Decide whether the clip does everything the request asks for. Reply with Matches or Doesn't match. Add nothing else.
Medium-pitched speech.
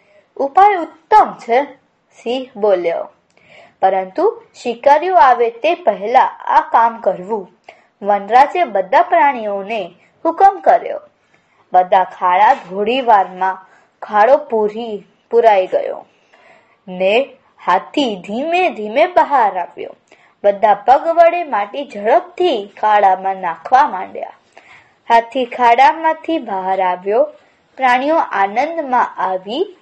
Doesn't match